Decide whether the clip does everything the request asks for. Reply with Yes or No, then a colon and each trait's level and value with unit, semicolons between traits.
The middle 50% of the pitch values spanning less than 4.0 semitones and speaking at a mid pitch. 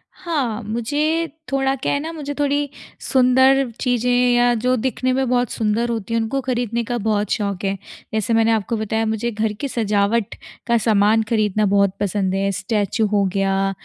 No: average, 3.5 semitones; high, 225 Hz